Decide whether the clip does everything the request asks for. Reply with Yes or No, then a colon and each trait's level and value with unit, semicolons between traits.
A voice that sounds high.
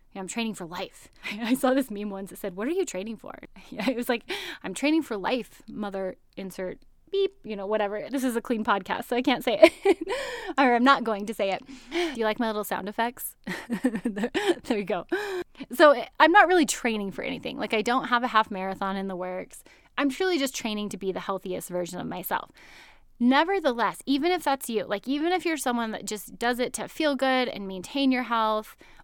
Yes: high, 240 Hz